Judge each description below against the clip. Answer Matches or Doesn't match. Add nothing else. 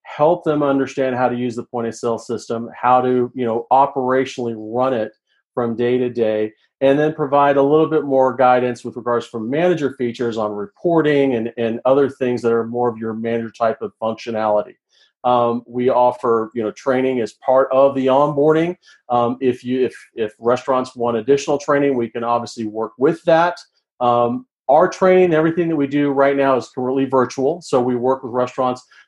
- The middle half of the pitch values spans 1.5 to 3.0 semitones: Matches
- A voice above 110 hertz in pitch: Matches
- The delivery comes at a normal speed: Matches